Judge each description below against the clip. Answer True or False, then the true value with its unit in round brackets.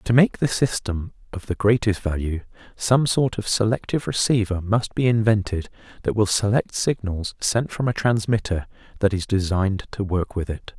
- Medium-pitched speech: False (105 Hz)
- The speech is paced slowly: False (175 wpm)